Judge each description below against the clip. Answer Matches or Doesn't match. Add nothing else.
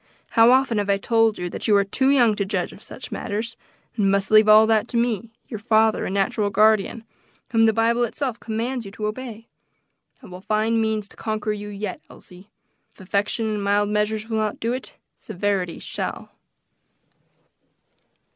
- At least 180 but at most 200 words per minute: Matches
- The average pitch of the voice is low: Doesn't match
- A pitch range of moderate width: Doesn't match